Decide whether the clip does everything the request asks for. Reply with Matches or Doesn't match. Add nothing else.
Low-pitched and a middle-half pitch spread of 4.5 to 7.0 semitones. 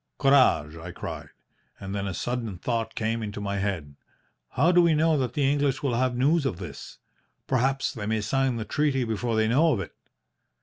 Matches